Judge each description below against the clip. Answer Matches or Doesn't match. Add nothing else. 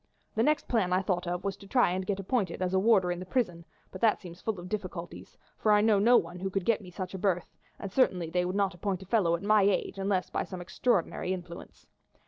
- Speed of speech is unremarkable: Doesn't match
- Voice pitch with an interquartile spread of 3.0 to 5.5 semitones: Doesn't match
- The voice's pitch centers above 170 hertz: Matches